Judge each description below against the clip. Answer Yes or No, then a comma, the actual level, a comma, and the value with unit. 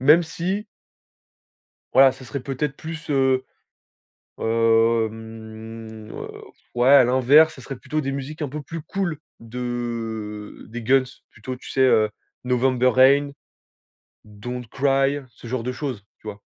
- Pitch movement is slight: No, average, 3.6 semitones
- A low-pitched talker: Yes, low, 130 Hz